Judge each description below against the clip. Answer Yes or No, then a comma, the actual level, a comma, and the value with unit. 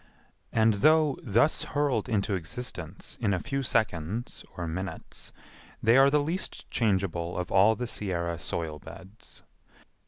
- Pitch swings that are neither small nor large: No, wide, 5.7 semitones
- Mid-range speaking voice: No, low, 105 Hz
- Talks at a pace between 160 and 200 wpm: No, slow, 135 wpm